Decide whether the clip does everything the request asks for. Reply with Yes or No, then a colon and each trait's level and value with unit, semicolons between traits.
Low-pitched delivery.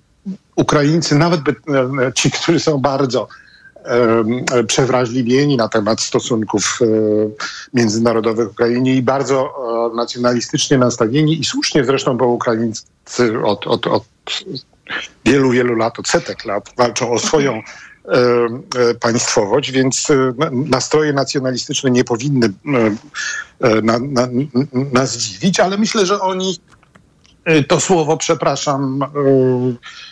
Yes: low, 130 Hz